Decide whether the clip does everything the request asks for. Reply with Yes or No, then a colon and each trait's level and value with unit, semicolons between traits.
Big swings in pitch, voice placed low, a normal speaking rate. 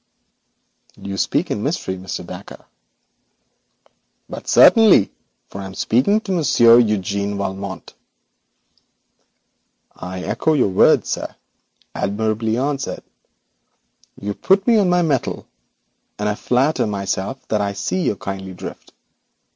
No: wide, 6.5 semitones; low, 105 Hz; slow, 120 wpm